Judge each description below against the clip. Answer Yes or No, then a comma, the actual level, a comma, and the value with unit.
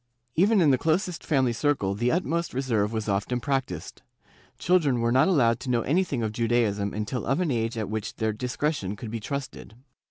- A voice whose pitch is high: No, low, 125 Hz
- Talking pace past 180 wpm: Yes, average, 200 wpm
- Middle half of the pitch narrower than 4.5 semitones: No, average, 4.9 semitones